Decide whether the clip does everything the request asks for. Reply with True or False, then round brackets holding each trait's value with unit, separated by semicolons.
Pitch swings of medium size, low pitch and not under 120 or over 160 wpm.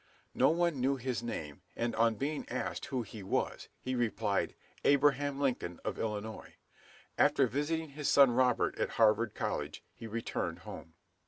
True (4.1 semitones; 120 Hz; 155 wpm)